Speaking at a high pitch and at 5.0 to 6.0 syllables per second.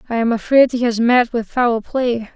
No: high, 235 Hz; 4.7 syllables/s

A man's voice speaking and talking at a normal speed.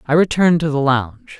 No: male; fast, 215 wpm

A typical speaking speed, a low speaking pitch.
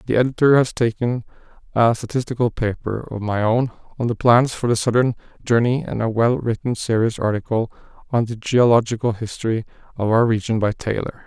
Yes: average, 170 wpm; low, 115 Hz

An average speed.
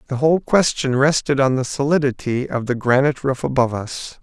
Yes: average, 185 wpm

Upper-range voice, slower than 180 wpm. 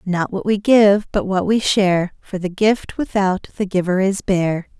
No: high, 195 Hz; average, 200 wpm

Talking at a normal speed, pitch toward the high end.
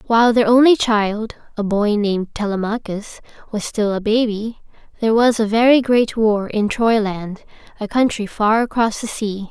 Yes: average, 165 wpm; high, 220 Hz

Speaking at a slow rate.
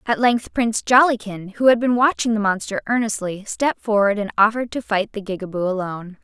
No: average, 190 wpm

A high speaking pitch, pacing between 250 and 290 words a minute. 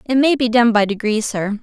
Yes: high, 230 Hz; fast, 260 wpm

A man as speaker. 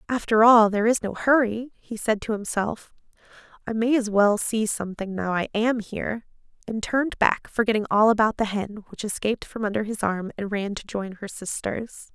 No: female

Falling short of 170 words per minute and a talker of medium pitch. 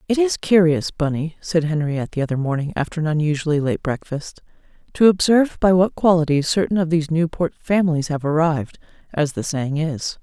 No: average, 175 wpm; medium, 160 Hz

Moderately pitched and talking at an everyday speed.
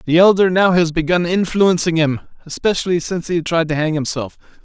Yes: medium, 170 Hz; average, 180 wpm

